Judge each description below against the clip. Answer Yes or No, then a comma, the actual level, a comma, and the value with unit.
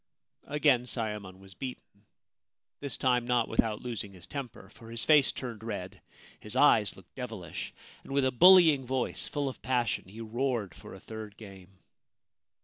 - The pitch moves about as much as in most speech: Yes, average, 4.2 semitones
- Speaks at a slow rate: No, average, 165 wpm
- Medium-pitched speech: No, low, 115 Hz